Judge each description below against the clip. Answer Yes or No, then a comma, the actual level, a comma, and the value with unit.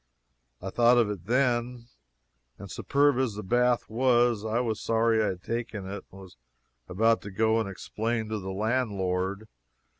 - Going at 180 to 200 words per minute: No, average, 170 wpm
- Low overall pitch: Yes, low, 110 Hz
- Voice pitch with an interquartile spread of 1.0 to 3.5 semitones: Yes, average, 3.2 semitones